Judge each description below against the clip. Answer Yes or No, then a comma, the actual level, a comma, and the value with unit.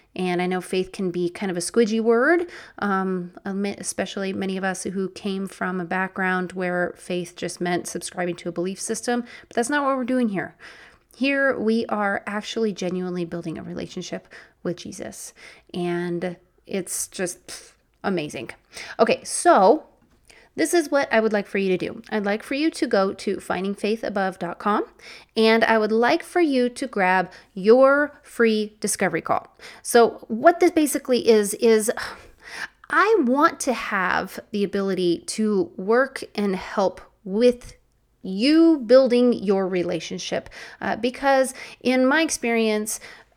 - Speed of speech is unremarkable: Yes, average, 150 wpm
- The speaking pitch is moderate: No, high, 205 Hz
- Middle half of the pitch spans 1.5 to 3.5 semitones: No, average, 5.0 semitones